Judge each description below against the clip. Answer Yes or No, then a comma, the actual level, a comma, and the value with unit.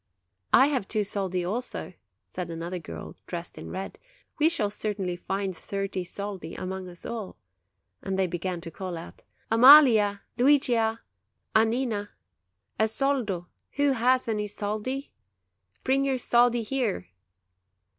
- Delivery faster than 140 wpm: No, slow, 135 wpm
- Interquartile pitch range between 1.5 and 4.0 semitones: No, average, 4.8 semitones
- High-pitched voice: Yes, high, 205 Hz